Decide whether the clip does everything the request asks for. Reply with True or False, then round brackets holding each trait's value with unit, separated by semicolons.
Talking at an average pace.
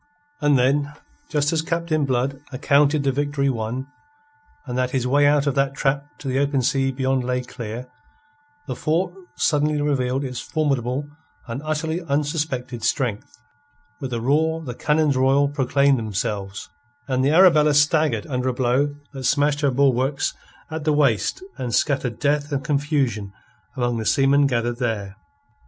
True (155 wpm)